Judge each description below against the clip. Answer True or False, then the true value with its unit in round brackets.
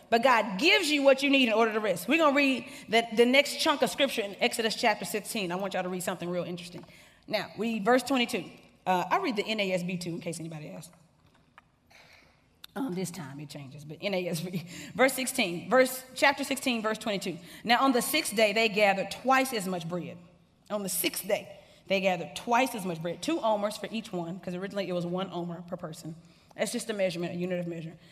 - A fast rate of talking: True (220 wpm)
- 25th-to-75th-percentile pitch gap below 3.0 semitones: False (5.3 semitones)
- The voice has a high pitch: True (195 Hz)